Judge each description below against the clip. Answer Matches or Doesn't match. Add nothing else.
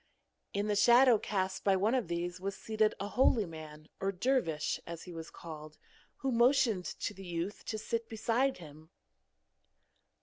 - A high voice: Matches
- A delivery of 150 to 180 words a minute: Matches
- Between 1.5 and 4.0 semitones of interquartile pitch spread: Doesn't match